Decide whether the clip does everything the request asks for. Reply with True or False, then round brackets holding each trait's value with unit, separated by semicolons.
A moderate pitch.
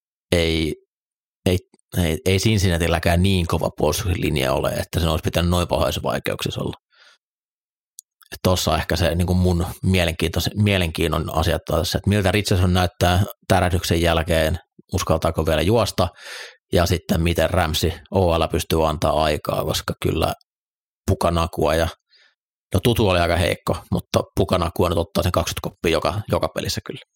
False (85 Hz)